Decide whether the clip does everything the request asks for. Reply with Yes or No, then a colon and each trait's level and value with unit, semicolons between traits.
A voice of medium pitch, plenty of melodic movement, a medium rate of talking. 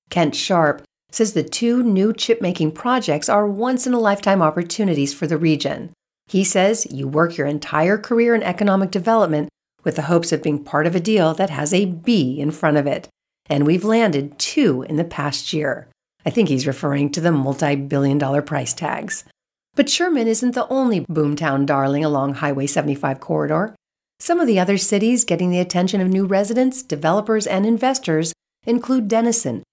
Yes: medium, 175 Hz; wide, 6.8 semitones; average, 185 wpm